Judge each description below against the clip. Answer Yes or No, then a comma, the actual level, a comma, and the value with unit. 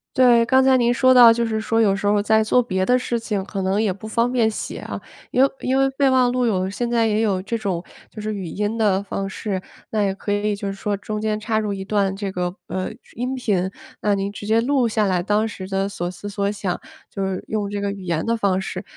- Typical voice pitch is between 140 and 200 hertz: No, high, 210 Hz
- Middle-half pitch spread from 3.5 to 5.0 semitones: No, average, 2.9 semitones